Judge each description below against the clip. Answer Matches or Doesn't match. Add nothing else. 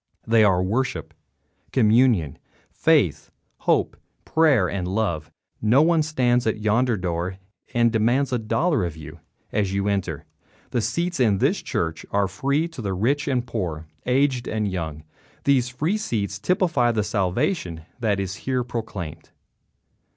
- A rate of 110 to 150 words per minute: Matches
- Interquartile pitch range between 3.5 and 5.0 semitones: Doesn't match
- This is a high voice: Doesn't match